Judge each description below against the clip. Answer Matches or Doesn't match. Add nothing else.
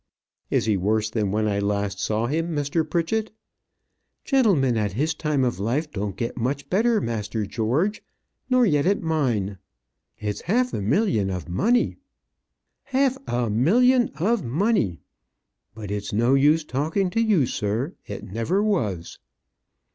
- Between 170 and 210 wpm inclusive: Doesn't match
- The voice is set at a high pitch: Doesn't match